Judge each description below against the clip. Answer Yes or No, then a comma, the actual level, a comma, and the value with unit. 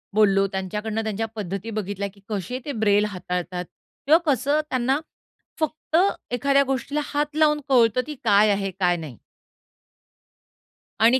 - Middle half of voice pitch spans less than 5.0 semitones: No, wide, 5.4 semitones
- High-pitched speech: Yes, high, 220 Hz